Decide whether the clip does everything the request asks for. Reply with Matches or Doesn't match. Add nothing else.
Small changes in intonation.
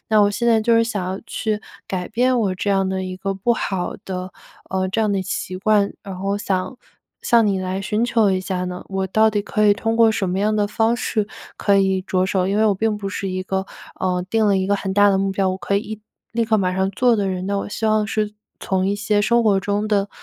Matches